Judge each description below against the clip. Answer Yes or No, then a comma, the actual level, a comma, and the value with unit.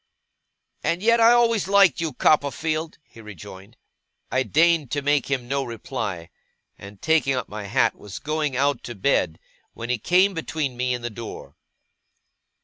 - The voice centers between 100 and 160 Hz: Yes, low, 135 Hz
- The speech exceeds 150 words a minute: Yes, average, 160 wpm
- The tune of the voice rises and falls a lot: Yes, wide, 5.7 semitones